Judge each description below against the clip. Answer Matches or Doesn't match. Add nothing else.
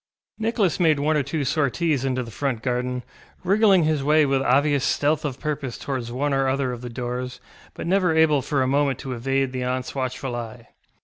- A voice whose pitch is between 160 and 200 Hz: Doesn't match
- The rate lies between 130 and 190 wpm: Doesn't match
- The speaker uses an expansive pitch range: Doesn't match